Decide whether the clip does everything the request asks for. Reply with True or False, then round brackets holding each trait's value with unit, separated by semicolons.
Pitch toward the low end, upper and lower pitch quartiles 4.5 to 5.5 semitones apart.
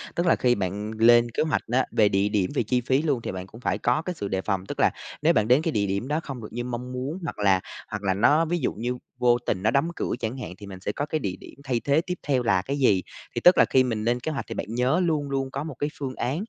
True (125 Hz; 5.2 semitones)